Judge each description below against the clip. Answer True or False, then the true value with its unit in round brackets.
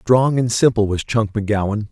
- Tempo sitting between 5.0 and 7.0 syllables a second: True (5.4 syllables/s)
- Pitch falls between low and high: False (110 Hz)